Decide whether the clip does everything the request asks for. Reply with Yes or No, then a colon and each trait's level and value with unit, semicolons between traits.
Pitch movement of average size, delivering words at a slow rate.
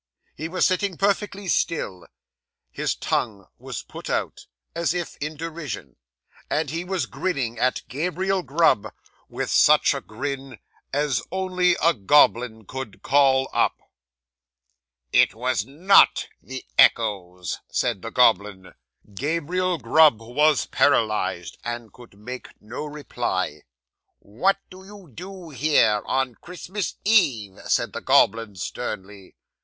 No: wide, 8.2 semitones; slow, 125 wpm